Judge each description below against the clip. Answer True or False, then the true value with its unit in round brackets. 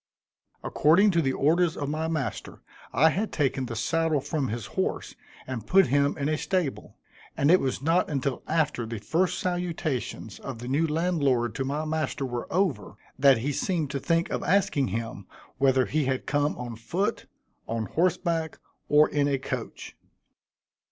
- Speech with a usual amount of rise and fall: True (3.9 semitones)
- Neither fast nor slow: True (170 wpm)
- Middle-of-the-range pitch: True (145 Hz)